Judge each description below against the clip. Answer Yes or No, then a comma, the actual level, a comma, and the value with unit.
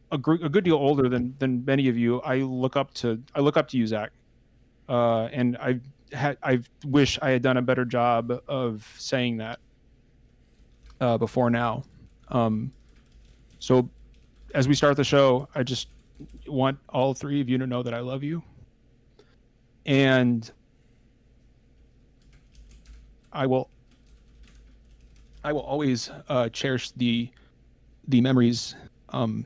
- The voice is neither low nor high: No, low, 125 Hz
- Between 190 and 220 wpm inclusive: No, average, 140 wpm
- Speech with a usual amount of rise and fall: No, narrow, 2.3 semitones